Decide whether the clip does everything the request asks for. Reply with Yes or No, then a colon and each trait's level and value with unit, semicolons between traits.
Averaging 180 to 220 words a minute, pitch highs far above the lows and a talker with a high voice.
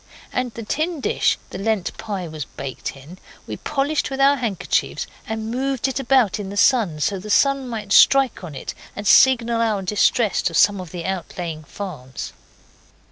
Yes: average, 185 wpm; wide, 6.0 semitones; high, 210 Hz